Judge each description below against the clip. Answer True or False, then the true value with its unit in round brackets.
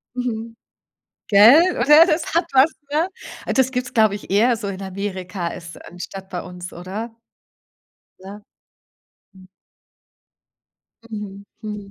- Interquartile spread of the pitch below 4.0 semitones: False (4.5 semitones)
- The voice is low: False (205 Hz)